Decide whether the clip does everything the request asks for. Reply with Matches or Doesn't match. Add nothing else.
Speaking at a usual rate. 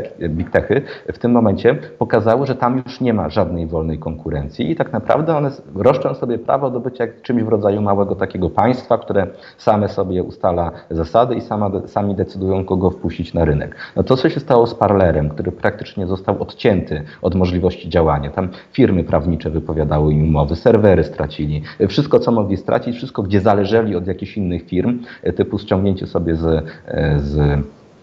Doesn't match